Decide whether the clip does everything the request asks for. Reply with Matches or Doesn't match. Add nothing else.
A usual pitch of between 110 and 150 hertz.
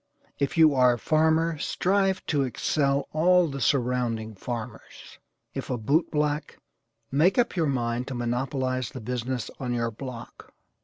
Matches